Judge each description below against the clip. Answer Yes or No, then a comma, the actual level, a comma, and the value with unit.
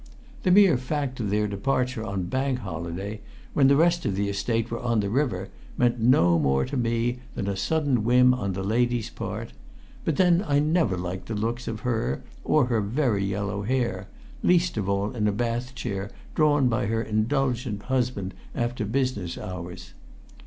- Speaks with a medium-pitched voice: No, low, 115 Hz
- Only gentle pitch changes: No, average, 4.4 semitones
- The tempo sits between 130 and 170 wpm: No, average, 180 wpm